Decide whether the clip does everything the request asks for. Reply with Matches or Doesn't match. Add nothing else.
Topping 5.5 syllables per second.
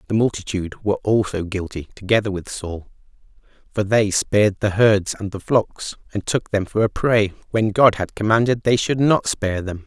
Doesn't match